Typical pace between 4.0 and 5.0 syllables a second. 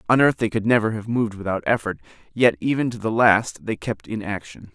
No: 5.8 syllables/s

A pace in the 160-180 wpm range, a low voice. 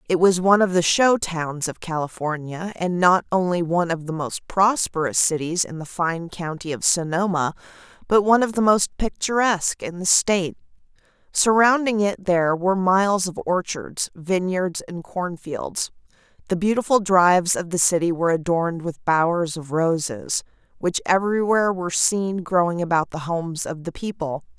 No: average, 165 wpm; medium, 180 Hz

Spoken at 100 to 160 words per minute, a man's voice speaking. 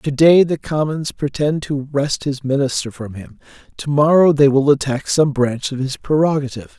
No: average, 185 wpm; male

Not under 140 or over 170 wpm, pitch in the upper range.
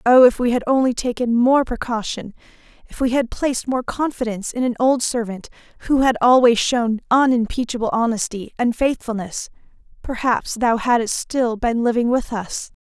Yes: average, 160 wpm; high, 240 Hz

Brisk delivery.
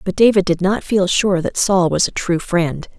Yes: fast, 240 wpm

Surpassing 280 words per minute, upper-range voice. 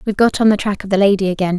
Yes: fast, 340 wpm; high, 200 Hz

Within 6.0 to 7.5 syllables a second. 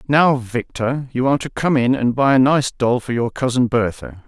No: 5.0 syllables/s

